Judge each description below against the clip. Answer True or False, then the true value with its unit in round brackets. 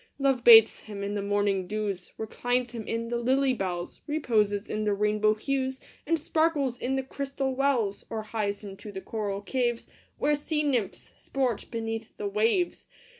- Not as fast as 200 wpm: True (175 wpm)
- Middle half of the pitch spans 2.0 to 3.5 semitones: False (4.4 semitones)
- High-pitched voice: True (230 Hz)